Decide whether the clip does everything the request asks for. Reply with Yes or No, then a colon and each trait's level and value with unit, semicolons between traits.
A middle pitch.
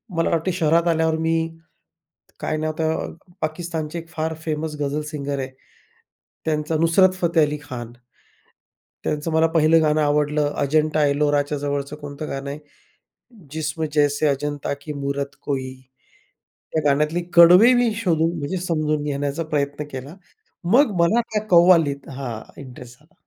Yes: medium, 150 Hz